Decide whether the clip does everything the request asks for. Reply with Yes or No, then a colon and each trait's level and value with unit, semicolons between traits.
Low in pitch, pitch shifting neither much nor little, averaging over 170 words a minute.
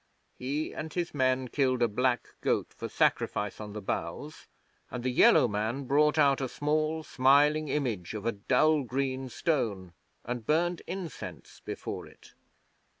No: low, 130 Hz; average, 4.1 semitones; average, 150 wpm